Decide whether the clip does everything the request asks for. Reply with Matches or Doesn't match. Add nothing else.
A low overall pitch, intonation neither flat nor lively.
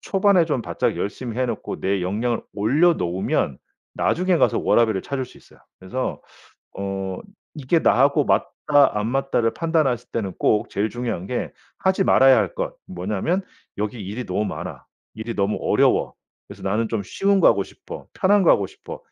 Doesn't match